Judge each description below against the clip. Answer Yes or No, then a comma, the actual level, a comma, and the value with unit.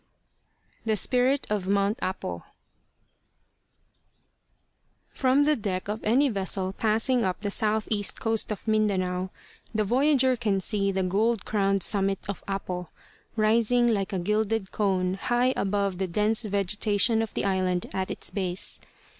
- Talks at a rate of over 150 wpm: No, average, 140 wpm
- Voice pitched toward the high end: Yes, high, 205 Hz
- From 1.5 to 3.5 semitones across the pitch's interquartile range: Yes, average, 2.7 semitones